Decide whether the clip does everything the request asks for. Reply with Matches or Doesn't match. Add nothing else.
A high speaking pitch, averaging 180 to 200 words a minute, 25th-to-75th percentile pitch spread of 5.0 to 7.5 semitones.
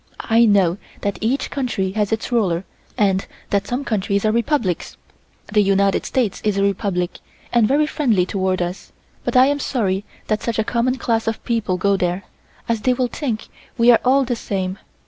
Doesn't match